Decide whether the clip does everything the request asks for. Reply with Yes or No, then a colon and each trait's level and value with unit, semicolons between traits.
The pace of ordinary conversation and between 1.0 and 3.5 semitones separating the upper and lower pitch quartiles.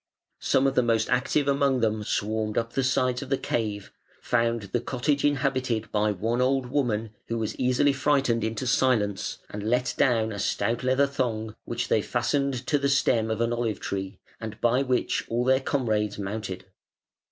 Yes: average, 180 wpm; average, 3.2 semitones